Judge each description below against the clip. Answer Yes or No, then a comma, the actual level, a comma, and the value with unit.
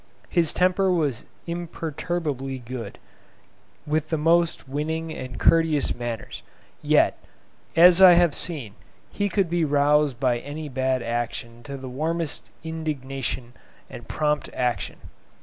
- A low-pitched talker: No, medium, 150 Hz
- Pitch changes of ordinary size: Yes, average, 4.2 semitones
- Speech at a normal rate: No, slow, 125 wpm